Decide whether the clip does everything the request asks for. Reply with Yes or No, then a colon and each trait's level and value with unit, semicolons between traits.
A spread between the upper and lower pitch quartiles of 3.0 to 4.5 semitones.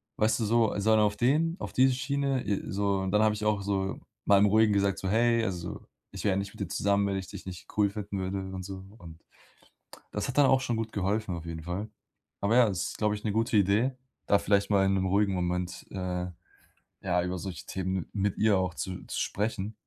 No: narrow, 2.5 semitones